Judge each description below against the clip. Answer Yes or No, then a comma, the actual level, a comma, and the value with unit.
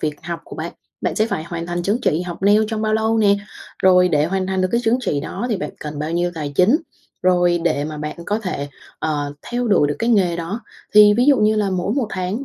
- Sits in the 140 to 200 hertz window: Yes, medium, 185 Hz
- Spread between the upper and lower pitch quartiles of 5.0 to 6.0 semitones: No, average, 4.6 semitones